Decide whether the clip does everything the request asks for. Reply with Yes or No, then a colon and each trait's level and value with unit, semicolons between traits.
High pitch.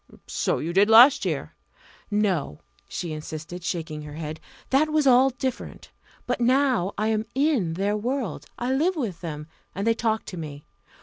Yes: high, 210 Hz